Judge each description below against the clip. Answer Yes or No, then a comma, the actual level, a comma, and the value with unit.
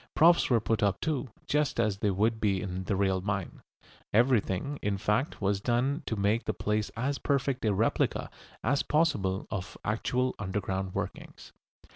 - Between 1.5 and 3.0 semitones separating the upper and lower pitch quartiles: No, average, 4.6 semitones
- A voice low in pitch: Yes, low, 105 Hz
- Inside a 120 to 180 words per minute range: Yes, average, 165 wpm